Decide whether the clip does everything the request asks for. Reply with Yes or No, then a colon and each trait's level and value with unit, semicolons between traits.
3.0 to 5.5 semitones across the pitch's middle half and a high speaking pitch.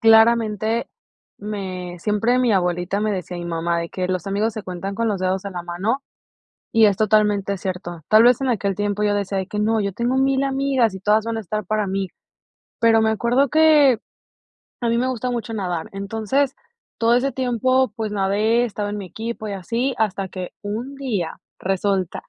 Yes: average, 3.4 semitones; high, 210 Hz